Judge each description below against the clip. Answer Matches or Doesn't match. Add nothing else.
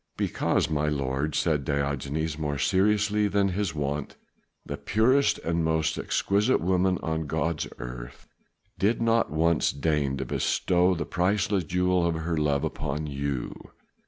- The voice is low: Matches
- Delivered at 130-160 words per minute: Matches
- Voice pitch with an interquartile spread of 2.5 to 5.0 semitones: Matches